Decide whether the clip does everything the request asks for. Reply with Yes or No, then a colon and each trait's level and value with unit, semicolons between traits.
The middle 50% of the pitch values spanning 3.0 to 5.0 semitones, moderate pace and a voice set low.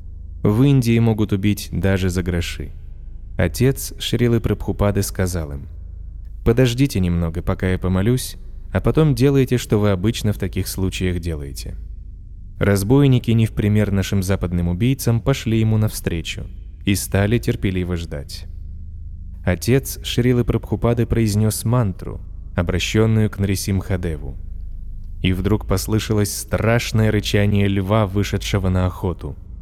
Yes: average, 4.0 semitones; average, 120 wpm; very low, 95 Hz